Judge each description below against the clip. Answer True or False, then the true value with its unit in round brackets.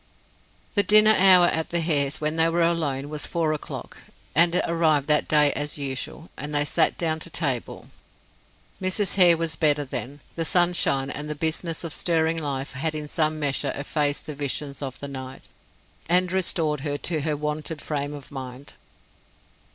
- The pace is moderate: True (175 wpm)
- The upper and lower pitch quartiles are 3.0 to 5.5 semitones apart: False (2.6 semitones)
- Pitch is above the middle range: False (155 Hz)